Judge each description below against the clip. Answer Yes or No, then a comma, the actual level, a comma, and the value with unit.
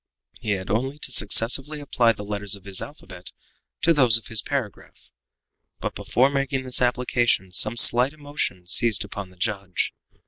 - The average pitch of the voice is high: No, low, 115 Hz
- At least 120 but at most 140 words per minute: No, average, 165 wpm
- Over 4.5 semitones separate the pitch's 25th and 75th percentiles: Yes, average, 4.9 semitones